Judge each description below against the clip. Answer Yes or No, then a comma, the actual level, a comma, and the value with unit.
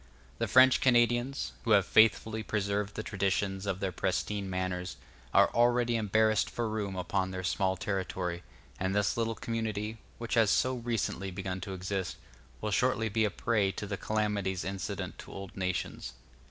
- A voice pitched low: Yes, low, 100 Hz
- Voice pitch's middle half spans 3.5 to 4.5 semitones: No, average, 2.9 semitones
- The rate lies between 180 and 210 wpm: No, average, 165 wpm